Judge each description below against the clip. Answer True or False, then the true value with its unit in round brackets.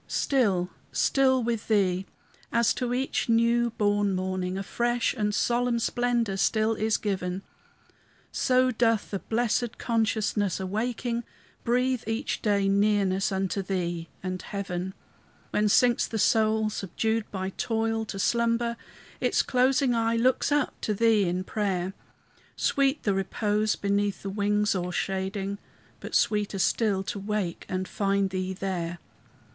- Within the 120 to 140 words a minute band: True (135 wpm)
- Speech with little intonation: False (3.3 semitones)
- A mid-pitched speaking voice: False (210 Hz)